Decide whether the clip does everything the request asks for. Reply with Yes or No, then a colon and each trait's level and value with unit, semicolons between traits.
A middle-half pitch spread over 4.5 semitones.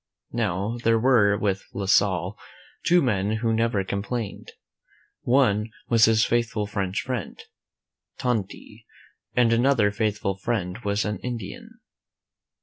No: average, 2.8 semitones